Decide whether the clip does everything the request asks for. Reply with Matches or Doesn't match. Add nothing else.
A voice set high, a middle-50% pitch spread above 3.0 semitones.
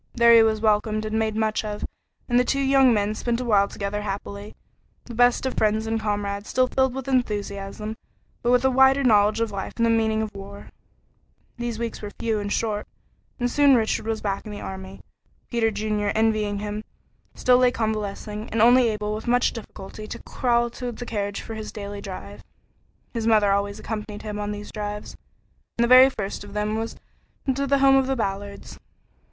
Doesn't match